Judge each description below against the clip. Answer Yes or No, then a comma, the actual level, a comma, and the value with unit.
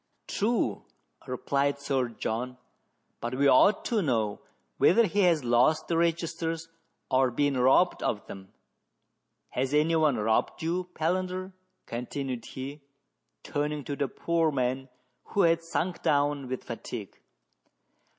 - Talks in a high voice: No, medium, 145 Hz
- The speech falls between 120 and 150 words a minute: Yes, average, 140 wpm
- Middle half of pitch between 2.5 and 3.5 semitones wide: No, average, 4.6 semitones